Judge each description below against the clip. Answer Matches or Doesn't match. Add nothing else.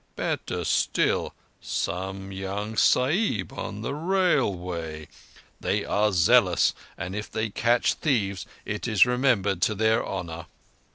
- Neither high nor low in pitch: Doesn't match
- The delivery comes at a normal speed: Doesn't match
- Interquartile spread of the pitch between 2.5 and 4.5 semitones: Matches